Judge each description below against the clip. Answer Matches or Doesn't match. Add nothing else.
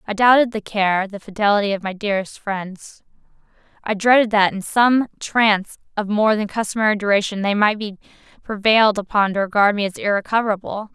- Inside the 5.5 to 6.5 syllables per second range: Matches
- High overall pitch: Matches